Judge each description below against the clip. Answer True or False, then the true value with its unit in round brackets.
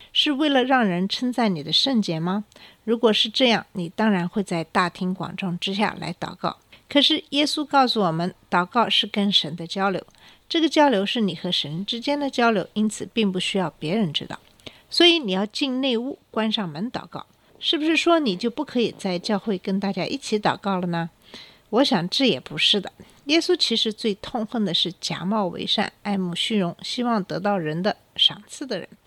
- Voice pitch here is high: True (210 Hz)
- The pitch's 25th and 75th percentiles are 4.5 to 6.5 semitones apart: True (5.2 semitones)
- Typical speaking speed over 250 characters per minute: True (285 characters per minute)